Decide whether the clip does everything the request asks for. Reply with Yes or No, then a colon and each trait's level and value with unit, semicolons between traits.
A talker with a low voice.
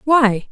No: very high, 250 Hz